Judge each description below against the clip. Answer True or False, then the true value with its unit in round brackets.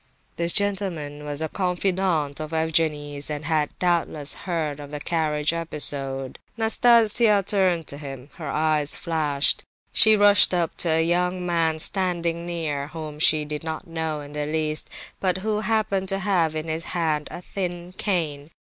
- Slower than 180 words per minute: True (160 wpm)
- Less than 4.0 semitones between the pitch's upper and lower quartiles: True (3.3 semitones)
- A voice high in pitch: False (160 Hz)